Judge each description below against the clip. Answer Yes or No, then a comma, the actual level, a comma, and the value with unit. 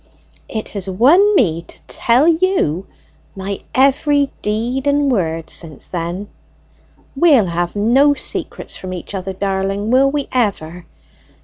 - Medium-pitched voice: No, high, 210 Hz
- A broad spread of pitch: Yes, wide, 6.9 semitones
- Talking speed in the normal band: No, slow, 130 wpm